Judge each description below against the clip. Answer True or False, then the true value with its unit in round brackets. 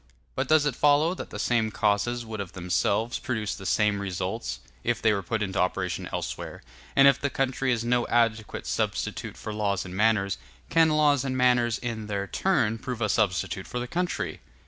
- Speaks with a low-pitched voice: True (115 Hz)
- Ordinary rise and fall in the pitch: True (4.0 semitones)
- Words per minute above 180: True (190 wpm)